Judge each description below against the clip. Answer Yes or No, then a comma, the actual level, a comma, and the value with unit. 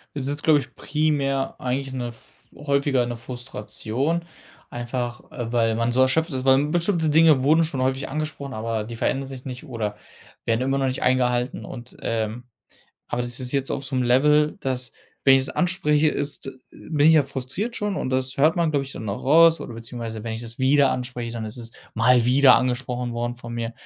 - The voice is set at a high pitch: No, low, 130 Hz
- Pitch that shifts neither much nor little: Yes, average, 3.1 semitones